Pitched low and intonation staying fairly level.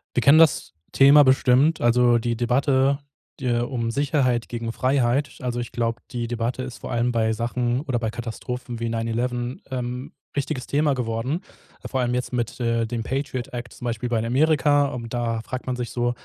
Yes: low, 120 Hz; narrow, 2.0 semitones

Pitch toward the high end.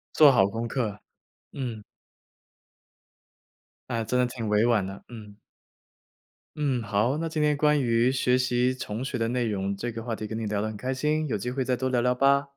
No: low, 120 Hz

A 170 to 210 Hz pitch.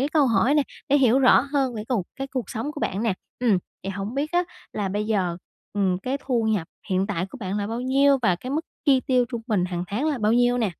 No: high, 235 Hz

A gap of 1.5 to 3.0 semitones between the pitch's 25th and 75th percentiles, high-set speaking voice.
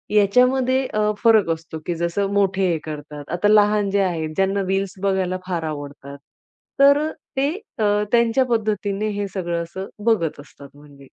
No: average, 4.2 semitones; high, 195 Hz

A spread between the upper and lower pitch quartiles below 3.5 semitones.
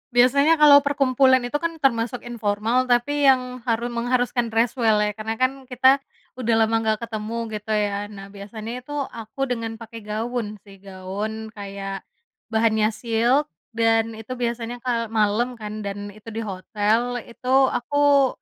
Yes: average, 2.9 semitones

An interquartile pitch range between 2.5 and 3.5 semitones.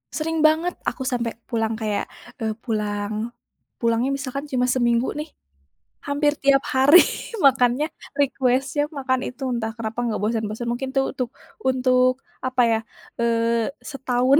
Yes: average, 2.9 semitones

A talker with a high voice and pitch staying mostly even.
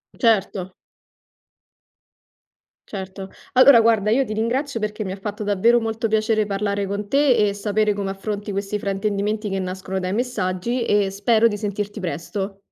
Yes: high, 205 Hz; narrow, 2.2 semitones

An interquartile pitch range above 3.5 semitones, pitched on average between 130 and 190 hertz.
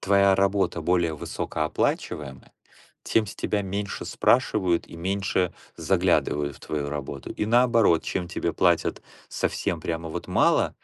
No: average, 3.9 semitones; very low, 90 Hz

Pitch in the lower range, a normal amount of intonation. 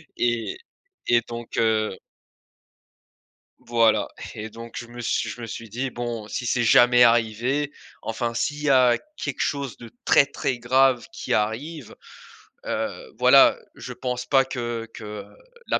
No: low, 120 Hz; narrow, 2.0 semitones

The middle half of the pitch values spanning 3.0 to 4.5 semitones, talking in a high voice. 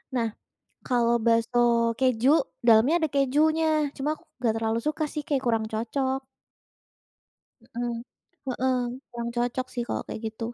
Yes: average, 3.3 semitones; high, 245 Hz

